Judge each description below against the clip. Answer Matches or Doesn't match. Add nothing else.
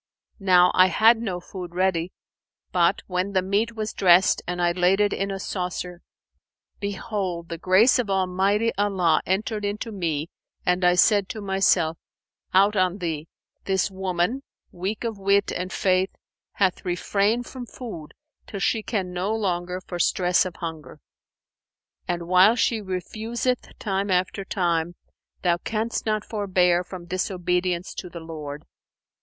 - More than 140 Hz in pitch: Matches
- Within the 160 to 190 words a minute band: Doesn't match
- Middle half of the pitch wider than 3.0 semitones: Doesn't match